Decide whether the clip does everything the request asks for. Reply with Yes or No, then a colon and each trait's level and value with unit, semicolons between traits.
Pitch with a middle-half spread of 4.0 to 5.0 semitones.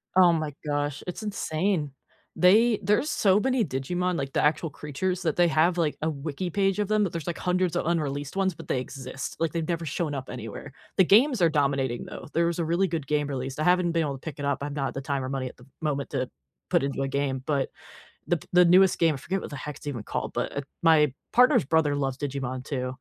Yes: average, 4.5 semitones